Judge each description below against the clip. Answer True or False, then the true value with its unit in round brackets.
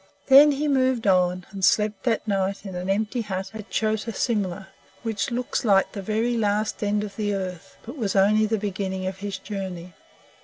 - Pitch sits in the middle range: False (205 Hz)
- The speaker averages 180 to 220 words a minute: True (195 wpm)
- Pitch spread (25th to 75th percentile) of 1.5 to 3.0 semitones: True (2.5 semitones)